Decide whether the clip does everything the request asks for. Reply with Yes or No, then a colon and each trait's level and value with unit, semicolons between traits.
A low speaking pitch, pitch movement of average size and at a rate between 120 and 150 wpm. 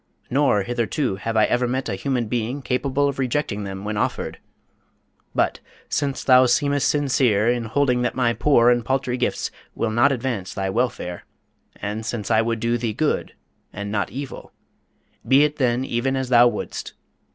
No: low, 120 Hz; average, 3.3 semitones; average, 170 wpm